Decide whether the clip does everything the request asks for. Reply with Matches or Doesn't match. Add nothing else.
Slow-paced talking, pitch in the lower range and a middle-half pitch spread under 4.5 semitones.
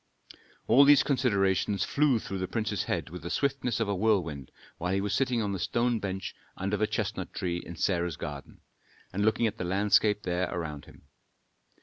Doesn't match